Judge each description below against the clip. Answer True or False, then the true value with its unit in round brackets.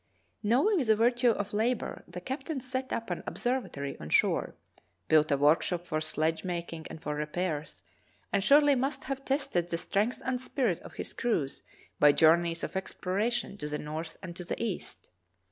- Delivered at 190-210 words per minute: False (180 wpm)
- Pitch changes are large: True (7.6 semitones)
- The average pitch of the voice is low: False (190 Hz)